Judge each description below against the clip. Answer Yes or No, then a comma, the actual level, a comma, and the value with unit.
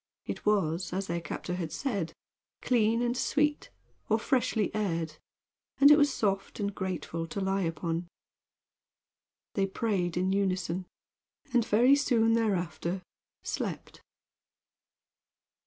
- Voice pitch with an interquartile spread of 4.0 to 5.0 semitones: Yes, average, 4.5 semitones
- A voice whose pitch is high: Yes, high, 195 Hz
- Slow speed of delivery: Yes, slow, 120 wpm